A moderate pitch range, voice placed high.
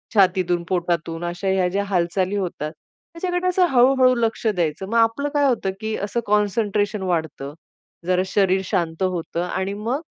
Yes: average, 4.3 semitones; high, 195 Hz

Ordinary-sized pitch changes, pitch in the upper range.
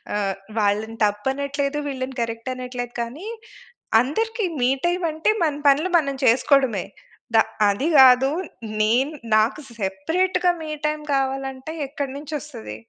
Yes: average, 4.6 semitones; very high, 265 Hz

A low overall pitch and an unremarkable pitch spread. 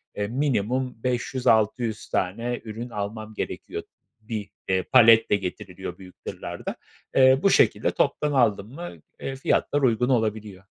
Yes: low, 115 Hz; average, 3.7 semitones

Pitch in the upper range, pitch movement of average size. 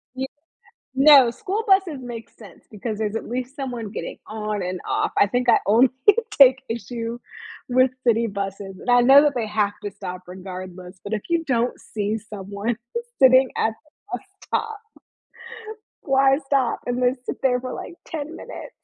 Yes: high, 240 Hz; average, 4.4 semitones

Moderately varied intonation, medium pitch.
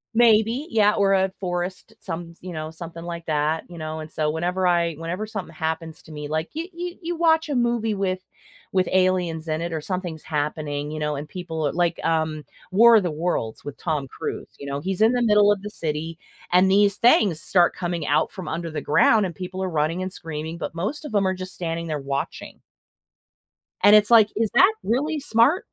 Yes: average, 4.6 semitones; medium, 175 Hz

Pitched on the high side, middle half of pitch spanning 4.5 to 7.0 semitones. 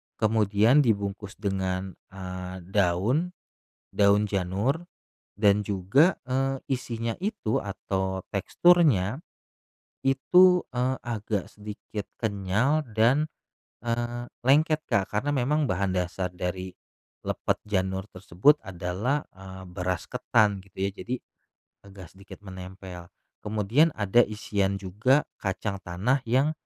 No: low, 105 Hz; average, 4.9 semitones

